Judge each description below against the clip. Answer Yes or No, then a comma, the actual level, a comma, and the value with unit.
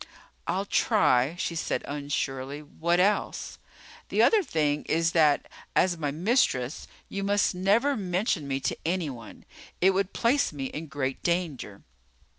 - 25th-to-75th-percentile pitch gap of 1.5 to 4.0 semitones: No, average, 5.3 semitones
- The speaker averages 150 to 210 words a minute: No, average, 140 wpm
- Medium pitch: Yes, medium, 165 Hz